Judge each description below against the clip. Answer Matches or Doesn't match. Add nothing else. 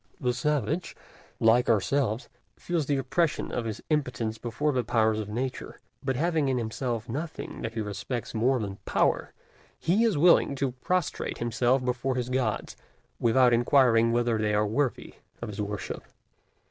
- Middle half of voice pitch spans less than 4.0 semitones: Matches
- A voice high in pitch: Doesn't match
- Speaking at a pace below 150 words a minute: Doesn't match